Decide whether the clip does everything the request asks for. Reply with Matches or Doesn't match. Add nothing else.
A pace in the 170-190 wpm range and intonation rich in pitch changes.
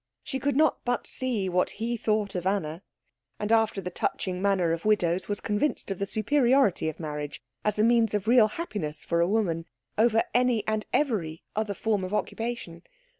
Doesn't match